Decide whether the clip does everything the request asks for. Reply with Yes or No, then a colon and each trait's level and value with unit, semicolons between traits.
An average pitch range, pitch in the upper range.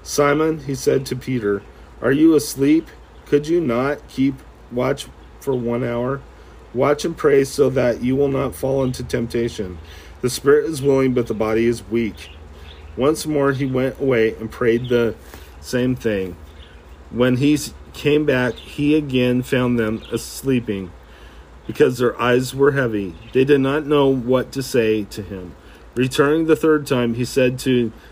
No: average, 4.2 semitones; low, 125 Hz